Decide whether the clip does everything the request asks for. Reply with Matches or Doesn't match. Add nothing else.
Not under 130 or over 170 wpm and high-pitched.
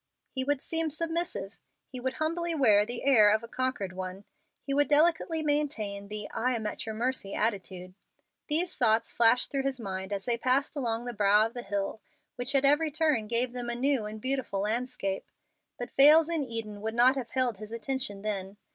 Doesn't match